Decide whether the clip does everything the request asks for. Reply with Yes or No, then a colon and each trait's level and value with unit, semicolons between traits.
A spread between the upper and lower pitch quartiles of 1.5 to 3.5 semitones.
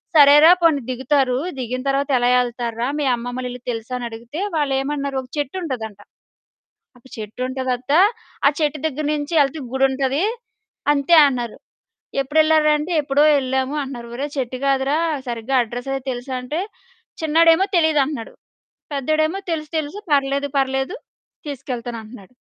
Yes: average, 2.9 semitones